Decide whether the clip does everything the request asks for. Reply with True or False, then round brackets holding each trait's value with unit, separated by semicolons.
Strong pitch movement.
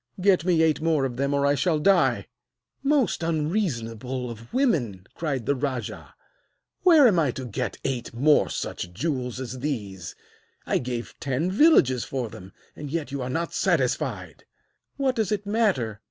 True (5.9 semitones)